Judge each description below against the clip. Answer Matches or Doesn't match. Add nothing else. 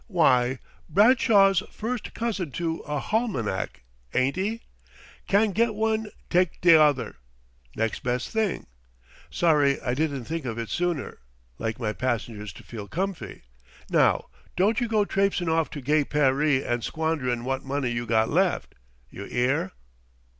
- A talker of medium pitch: Matches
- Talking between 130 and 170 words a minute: Matches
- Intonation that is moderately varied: Doesn't match